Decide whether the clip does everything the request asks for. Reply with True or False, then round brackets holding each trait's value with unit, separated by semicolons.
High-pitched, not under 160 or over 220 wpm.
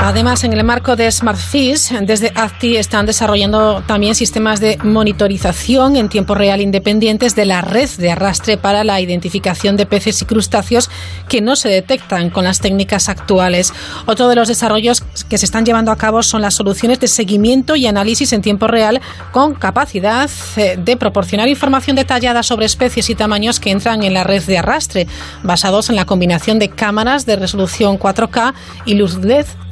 True (215 Hz; 175 wpm)